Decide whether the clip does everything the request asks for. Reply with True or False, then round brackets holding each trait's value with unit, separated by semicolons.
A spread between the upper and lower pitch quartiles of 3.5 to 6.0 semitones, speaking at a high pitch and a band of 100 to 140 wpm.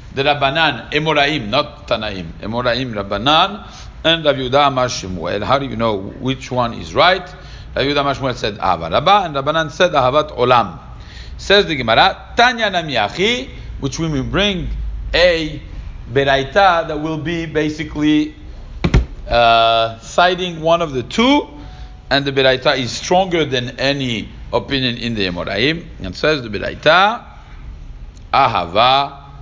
False (4.3 semitones; 140 Hz; 135 wpm)